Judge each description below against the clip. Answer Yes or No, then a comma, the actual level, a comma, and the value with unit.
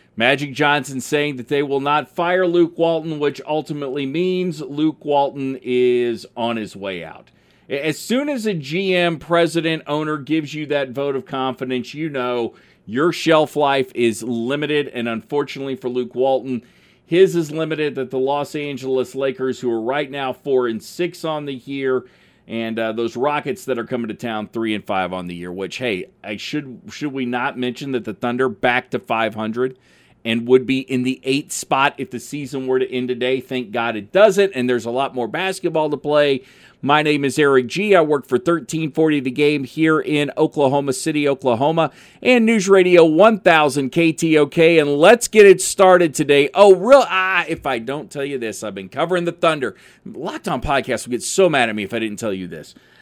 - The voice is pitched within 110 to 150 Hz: Yes, medium, 140 Hz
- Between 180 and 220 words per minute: Yes, average, 200 wpm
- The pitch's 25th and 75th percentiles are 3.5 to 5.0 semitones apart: Yes, average, 4.1 semitones